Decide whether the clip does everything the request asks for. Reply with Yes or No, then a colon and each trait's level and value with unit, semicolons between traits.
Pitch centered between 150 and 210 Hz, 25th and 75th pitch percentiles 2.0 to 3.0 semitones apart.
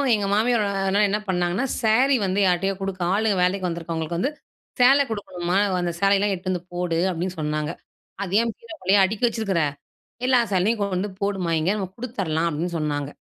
No: high, 190 Hz; average, 3.4 semitones